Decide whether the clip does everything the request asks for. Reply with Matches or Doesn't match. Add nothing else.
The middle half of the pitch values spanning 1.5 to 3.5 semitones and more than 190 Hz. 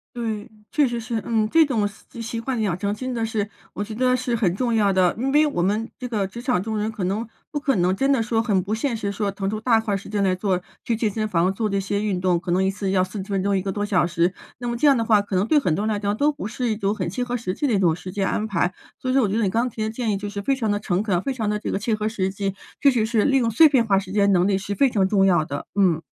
Matches